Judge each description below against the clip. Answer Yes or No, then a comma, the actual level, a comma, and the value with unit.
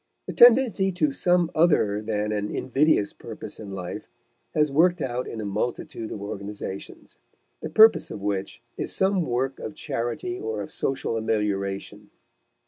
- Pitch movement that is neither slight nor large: No, wide, 7.4 semitones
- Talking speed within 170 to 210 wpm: No, average, 150 wpm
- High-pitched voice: No, low, 115 Hz